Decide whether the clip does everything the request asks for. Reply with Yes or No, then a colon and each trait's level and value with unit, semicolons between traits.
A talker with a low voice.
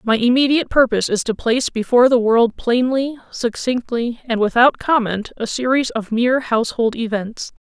No: high, 240 Hz